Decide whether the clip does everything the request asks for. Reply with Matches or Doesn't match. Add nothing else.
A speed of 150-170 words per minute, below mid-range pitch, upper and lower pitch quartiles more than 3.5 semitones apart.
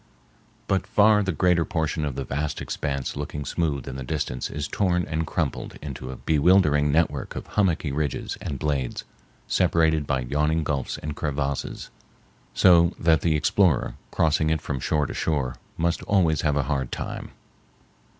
Doesn't match